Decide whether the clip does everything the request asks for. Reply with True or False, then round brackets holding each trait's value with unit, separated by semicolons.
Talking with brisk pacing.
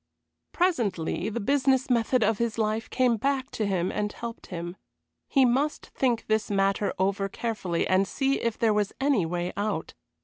False (170 wpm)